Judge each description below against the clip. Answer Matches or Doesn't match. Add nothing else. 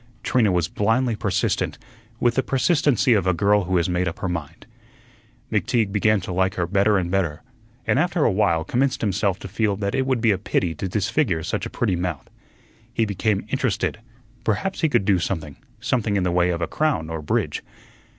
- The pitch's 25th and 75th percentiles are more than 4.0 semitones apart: Matches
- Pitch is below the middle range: Matches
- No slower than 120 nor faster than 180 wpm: Doesn't match